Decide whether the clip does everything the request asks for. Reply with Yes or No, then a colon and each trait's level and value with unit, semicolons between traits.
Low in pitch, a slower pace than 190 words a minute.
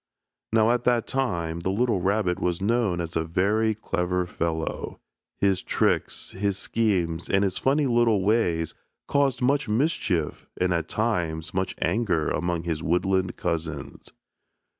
Yes: very low, 95 Hz; average, 140 wpm